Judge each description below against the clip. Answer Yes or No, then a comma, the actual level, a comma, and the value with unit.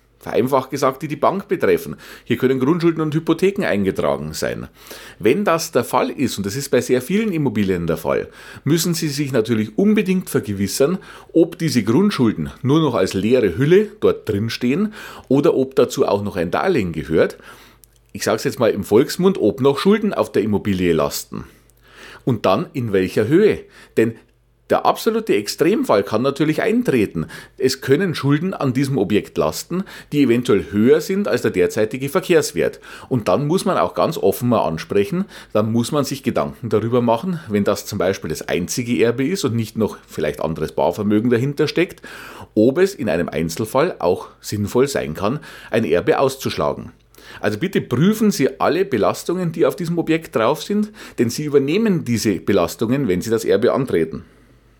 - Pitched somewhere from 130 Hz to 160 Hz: Yes, medium, 140 Hz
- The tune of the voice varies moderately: No, wide, 8.9 semitones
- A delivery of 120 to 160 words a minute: No, average, 175 wpm